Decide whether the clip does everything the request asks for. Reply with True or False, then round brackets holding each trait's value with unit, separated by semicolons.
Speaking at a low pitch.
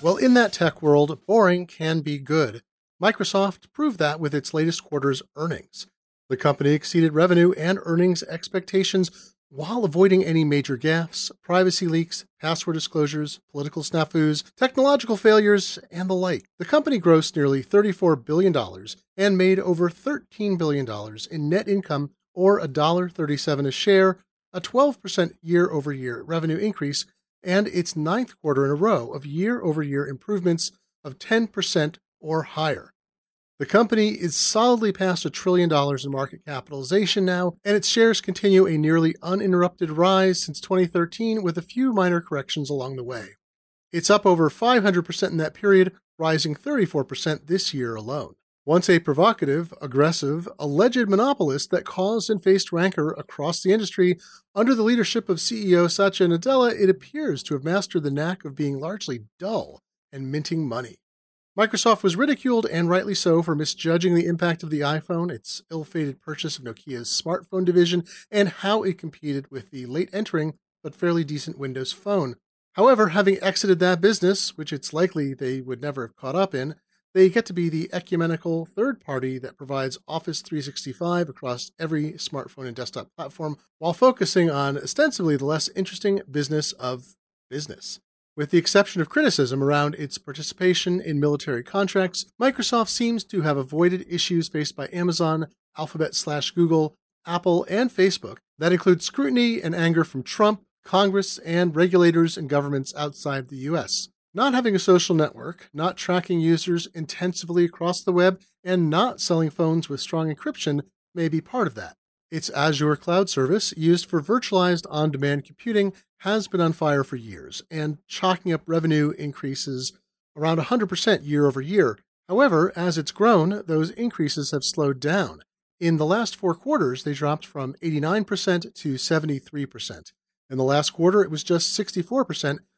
False (170 Hz)